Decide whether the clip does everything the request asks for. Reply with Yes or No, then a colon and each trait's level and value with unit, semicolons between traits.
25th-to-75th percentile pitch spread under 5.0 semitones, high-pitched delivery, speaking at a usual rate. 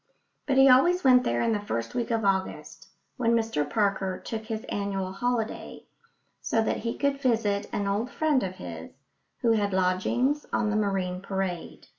Yes: average, 4.1 semitones; high, 210 Hz; average, 175 wpm